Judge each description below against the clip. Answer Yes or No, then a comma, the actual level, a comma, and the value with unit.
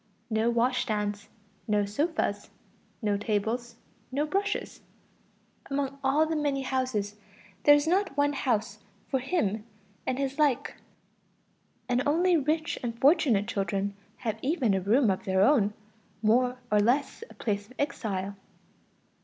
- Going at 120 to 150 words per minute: Yes, slow, 135 wpm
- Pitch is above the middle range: Yes, very high, 250 Hz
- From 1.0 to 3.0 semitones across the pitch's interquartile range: No, wide, 5.6 semitones